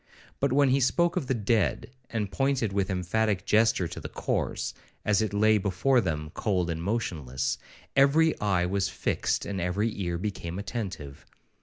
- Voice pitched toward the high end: No, low, 100 Hz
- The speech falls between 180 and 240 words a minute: No, average, 165 wpm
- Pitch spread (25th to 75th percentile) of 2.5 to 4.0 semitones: No, average, 4.6 semitones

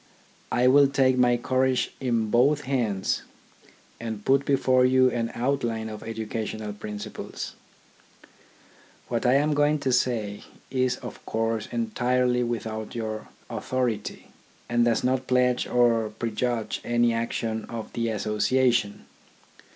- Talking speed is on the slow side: Yes, slow, 125 wpm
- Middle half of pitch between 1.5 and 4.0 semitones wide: Yes, narrow, 2.5 semitones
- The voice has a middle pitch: No, low, 120 Hz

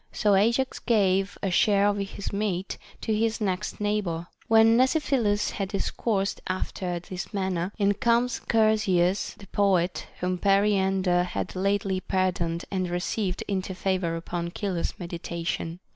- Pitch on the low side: No, high, 195 Hz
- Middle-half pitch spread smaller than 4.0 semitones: Yes, narrow, 2.5 semitones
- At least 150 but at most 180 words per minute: No, average, 140 wpm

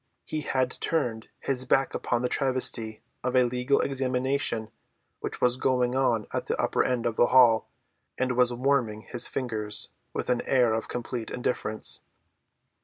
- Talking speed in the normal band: Yes, average, 160 wpm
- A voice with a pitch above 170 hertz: No, low, 125 Hz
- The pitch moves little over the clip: Yes, narrow, 1.9 semitones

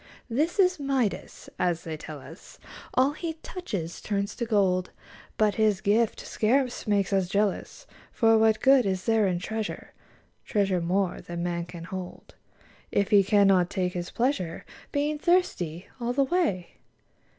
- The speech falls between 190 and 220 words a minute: No, average, 150 wpm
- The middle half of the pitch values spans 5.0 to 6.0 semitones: Yes, wide, 5.4 semitones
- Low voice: No, high, 205 Hz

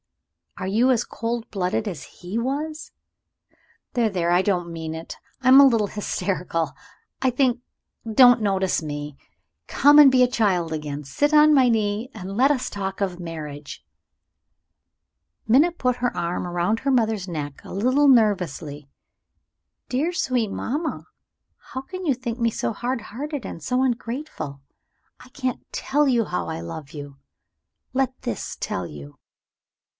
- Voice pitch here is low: No, high, 220 Hz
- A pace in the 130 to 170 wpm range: Yes, average, 155 wpm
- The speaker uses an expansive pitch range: Yes, wide, 7.0 semitones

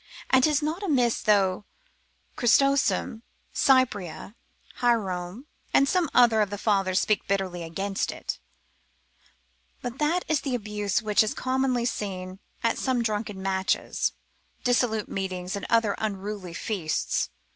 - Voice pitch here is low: No, high, 215 Hz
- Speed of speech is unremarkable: No, slow, 125 wpm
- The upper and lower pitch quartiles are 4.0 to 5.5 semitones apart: Yes, average, 4.5 semitones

